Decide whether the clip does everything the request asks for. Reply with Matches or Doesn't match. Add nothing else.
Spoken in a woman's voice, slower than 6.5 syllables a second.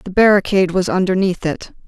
Matches